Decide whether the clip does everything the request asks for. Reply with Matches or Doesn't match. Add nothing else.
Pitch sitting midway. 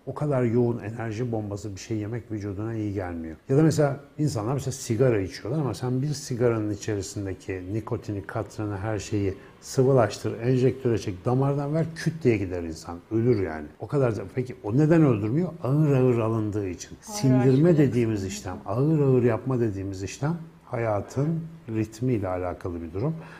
Doesn't match